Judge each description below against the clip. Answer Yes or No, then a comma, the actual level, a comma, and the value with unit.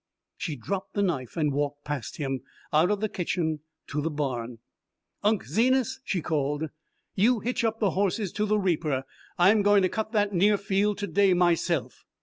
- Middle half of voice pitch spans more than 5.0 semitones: Yes, wide, 5.6 semitones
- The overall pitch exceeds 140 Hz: Yes, medium, 185 Hz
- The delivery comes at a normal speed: Yes, average, 180 wpm